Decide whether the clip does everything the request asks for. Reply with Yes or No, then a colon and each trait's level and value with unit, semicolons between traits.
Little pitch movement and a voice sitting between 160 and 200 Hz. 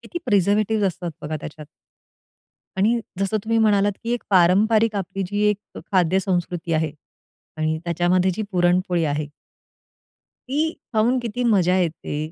No: average, 3.9 semitones; high, 190 Hz